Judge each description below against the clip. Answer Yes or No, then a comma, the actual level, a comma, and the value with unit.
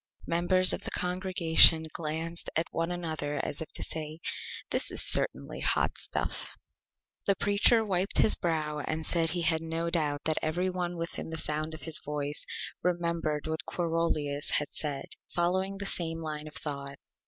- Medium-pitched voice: Yes, medium, 165 Hz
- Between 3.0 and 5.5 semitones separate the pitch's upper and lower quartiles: No, narrow, 2.4 semitones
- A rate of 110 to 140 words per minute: No, average, 165 wpm